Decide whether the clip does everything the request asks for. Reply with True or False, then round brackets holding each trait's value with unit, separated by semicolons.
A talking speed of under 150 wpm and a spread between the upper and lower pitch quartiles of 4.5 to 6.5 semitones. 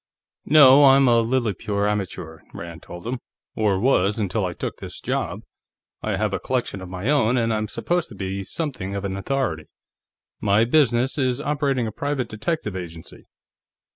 False (170 wpm; 5.4 semitones)